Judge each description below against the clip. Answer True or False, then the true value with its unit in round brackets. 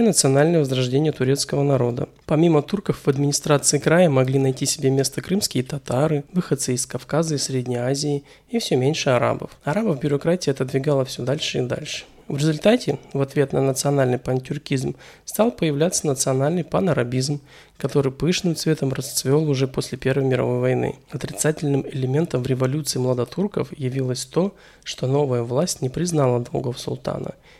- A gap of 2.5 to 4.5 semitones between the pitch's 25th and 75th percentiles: True (2.9 semitones)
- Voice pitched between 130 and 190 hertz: True (140 Hz)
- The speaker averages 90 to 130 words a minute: False (145 wpm)